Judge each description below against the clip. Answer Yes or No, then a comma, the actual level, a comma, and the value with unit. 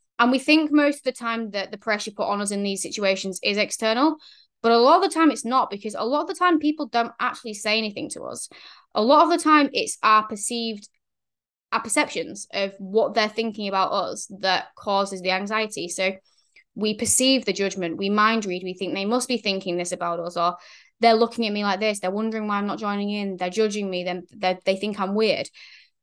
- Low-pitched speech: No, high, 215 Hz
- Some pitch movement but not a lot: Yes, average, 3.3 semitones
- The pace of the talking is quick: Yes, fast, 225 wpm